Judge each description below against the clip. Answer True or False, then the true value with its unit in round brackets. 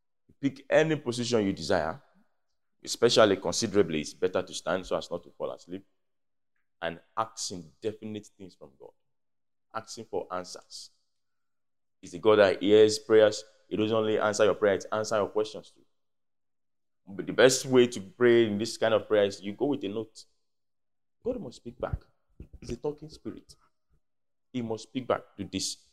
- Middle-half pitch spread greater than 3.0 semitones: True (3.9 semitones)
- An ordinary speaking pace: True (170 wpm)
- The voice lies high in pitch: False (110 Hz)